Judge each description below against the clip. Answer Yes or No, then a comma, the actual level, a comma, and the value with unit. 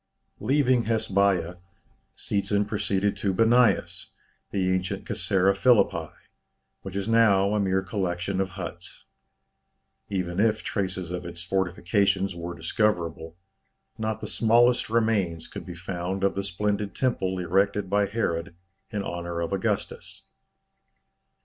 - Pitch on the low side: Yes, very low, 95 Hz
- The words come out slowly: Yes, slow, 125 wpm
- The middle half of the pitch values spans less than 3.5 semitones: Yes, average, 2.8 semitones